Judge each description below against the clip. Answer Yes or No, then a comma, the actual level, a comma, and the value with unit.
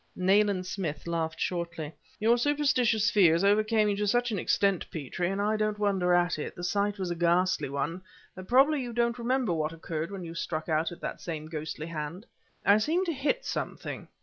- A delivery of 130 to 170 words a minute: No, average, 200 wpm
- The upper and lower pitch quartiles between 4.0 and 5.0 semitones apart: Yes, average, 4.4 semitones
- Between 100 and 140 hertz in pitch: No, high, 190 Hz